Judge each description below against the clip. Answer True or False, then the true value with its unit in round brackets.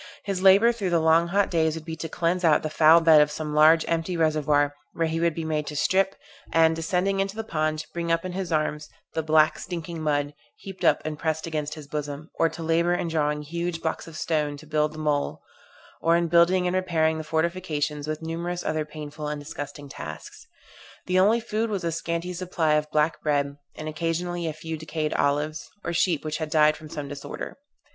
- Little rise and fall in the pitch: True (2.0 semitones)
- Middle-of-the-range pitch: True (160 Hz)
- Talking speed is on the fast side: True (215 wpm)